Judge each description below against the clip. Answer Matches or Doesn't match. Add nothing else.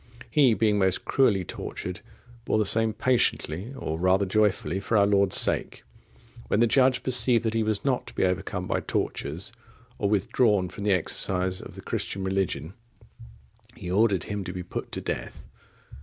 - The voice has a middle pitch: Doesn't match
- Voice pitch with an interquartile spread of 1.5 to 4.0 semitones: Matches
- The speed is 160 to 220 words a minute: Matches